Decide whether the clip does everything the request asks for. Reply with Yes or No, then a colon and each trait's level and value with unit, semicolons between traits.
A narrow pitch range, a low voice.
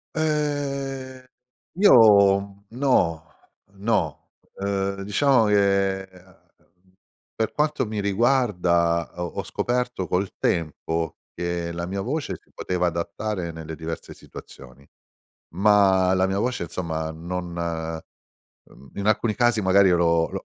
No: average, 4.6 semitones; very low, 95 Hz